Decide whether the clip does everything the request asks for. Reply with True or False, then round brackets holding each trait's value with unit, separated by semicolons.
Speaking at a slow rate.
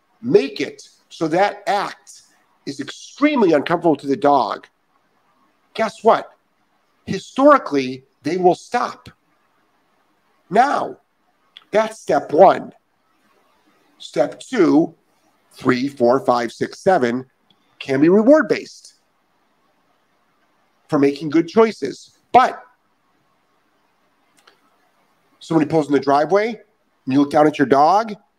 True (105 wpm)